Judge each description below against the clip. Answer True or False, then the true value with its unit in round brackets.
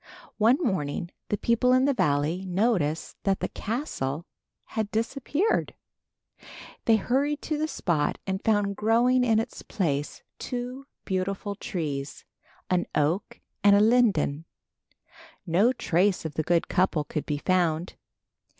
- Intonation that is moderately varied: False (6.5 semitones)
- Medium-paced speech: False (130 wpm)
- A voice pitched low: False (200 Hz)